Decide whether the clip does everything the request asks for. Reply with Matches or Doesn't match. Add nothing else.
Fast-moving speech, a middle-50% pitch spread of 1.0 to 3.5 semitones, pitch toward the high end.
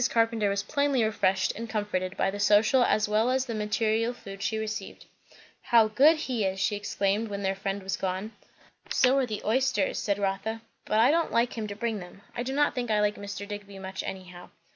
Matches